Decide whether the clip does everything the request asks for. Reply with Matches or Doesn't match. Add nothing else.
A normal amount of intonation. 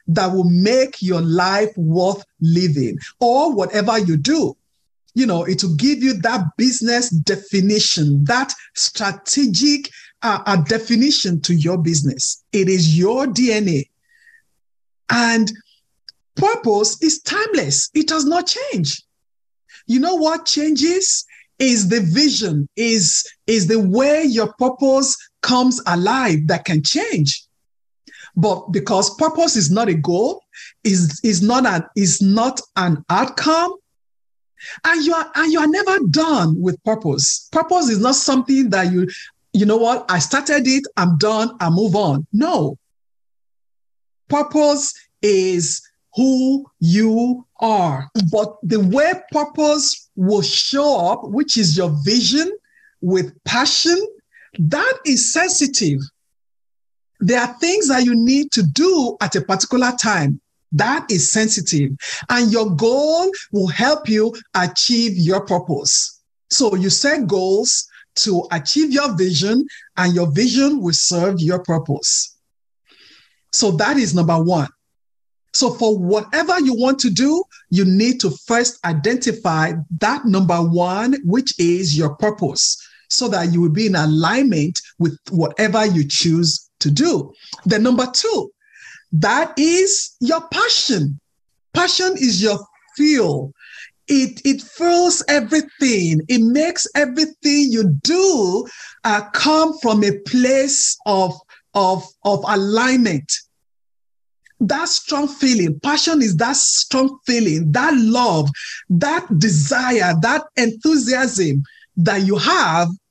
Doesn't match